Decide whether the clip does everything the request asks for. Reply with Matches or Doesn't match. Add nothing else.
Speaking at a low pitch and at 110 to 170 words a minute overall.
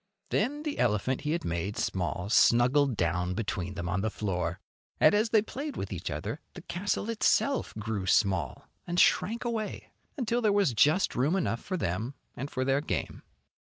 Doesn't match